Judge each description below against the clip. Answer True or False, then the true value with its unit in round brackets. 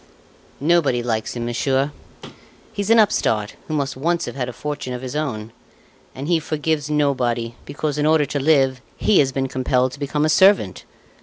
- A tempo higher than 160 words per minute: True (180 wpm)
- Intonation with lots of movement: False (3.5 semitones)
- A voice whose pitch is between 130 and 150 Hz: True (140 Hz)